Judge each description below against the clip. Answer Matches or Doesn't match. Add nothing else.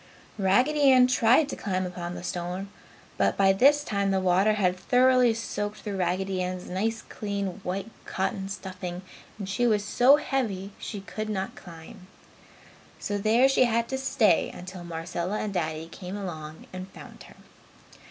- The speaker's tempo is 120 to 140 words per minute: Doesn't match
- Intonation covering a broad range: Doesn't match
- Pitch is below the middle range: Doesn't match